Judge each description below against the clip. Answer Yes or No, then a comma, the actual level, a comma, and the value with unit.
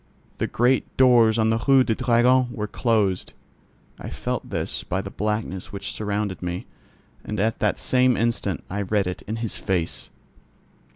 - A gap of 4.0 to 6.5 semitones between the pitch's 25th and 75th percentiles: No, average, 3.2 semitones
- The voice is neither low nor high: No, low, 110 Hz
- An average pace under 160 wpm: No, average, 165 wpm